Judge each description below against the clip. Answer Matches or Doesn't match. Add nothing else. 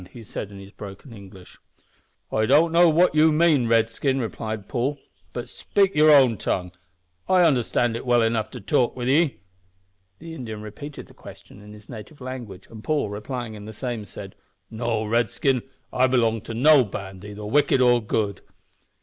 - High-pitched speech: Doesn't match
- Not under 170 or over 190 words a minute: Matches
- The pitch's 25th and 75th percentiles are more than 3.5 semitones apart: Matches